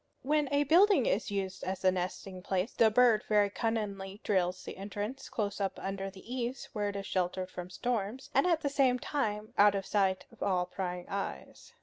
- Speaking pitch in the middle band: No, high, 205 Hz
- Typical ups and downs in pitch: Yes, average, 4.5 semitones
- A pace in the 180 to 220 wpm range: Yes, average, 200 wpm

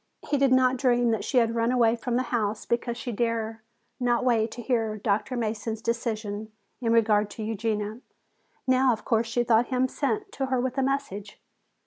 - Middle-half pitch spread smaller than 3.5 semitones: Yes, narrow, 2.4 semitones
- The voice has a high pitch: Yes, high, 235 Hz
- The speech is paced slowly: No, average, 190 wpm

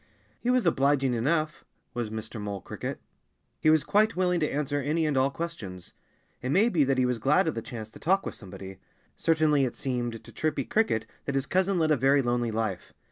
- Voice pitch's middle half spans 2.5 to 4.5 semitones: No, wide, 5.4 semitones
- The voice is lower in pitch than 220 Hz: Yes, medium, 140 Hz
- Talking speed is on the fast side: Yes, fast, 210 wpm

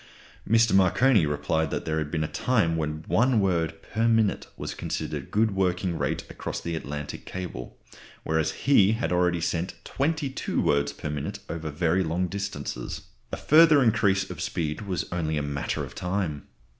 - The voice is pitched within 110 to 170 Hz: No, very low, 90 Hz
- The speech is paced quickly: No, average, 175 wpm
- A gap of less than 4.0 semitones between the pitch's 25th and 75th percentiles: No, average, 5.0 semitones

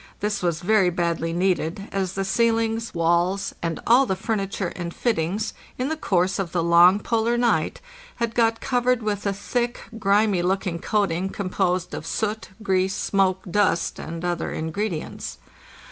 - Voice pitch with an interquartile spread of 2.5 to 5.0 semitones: Yes, average, 3.8 semitones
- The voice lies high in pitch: Yes, high, 195 Hz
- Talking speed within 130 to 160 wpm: Yes, average, 155 wpm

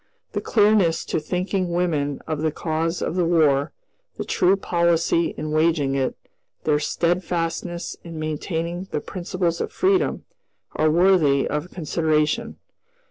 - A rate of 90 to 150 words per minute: Yes, slow, 135 wpm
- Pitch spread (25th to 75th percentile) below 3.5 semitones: Yes, narrow, 2.5 semitones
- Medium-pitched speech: Yes, medium, 165 Hz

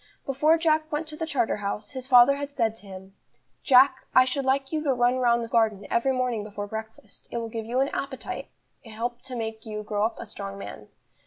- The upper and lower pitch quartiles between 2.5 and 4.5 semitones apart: Yes, average, 3.6 semitones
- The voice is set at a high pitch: Yes, high, 240 Hz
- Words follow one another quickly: Yes, fast, 230 wpm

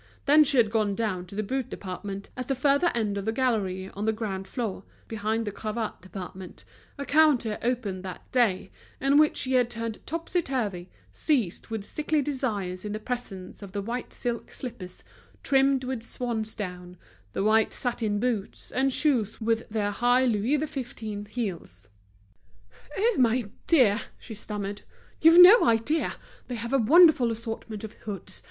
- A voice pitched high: Yes, high, 225 Hz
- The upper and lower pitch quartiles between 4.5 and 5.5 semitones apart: No, average, 4.1 semitones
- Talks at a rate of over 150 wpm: Yes, average, 165 wpm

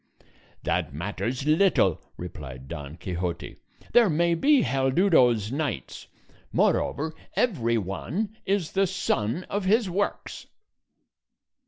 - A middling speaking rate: No, slow, 105 wpm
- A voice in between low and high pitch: Yes, medium, 145 Hz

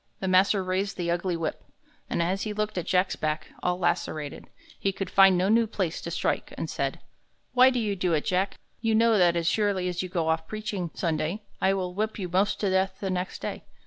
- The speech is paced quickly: Yes, fast, 225 wpm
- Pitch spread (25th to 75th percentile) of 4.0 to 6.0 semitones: No, narrow, 2.5 semitones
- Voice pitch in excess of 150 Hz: Yes, medium, 185 Hz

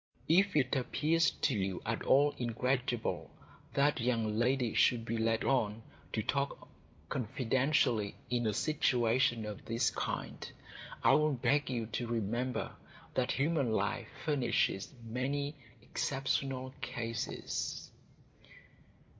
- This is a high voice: No, low, 125 Hz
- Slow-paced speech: Yes, slow, 115 wpm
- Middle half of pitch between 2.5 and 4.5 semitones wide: Yes, average, 3.3 semitones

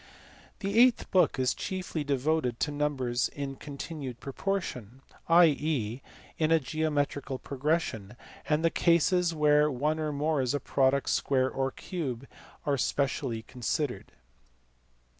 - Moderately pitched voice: Yes, medium, 145 Hz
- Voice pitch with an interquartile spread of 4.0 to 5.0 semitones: No, average, 3.3 semitones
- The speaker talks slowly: Yes, slow, 125 wpm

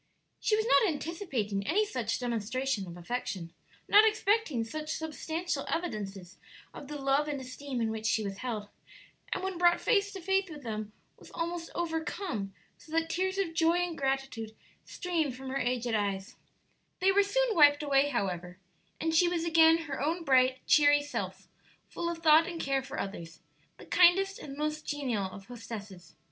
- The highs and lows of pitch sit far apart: Yes, wide, 7.1 semitones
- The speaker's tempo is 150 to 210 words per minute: Yes, average, 175 wpm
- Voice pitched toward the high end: Yes, very high, 290 Hz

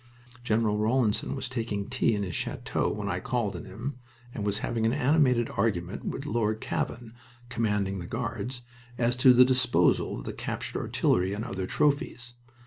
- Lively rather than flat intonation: No, average, 3.6 semitones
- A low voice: Yes, low, 115 Hz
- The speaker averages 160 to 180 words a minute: Yes, average, 170 wpm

